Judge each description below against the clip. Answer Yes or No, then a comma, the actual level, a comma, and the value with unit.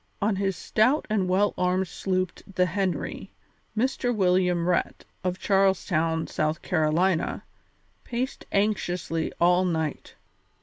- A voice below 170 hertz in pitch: No, medium, 185 Hz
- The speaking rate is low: Yes, slow, 120 wpm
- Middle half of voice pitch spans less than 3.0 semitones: Yes, narrow, 2.4 semitones